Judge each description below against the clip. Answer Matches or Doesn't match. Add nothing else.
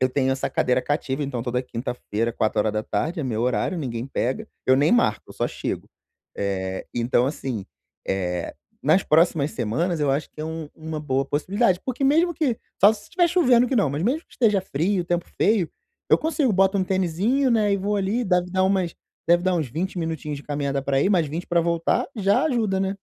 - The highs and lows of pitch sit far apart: Matches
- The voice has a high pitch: Doesn't match